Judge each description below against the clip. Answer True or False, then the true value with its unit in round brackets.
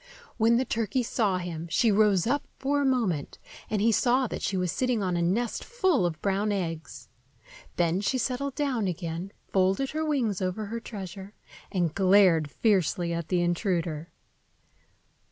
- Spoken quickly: False (165 wpm)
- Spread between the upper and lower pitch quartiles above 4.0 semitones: True (5.4 semitones)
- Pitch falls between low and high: False (200 Hz)